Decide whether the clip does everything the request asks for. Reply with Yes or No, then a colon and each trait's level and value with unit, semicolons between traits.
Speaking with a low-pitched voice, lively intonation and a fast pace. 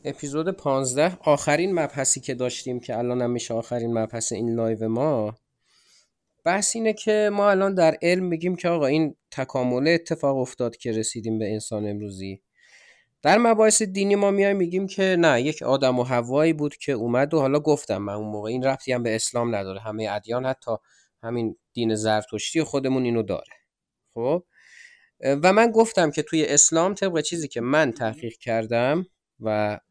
Yes: low, 130 Hz; wide, 6.1 semitones; fast, 165 wpm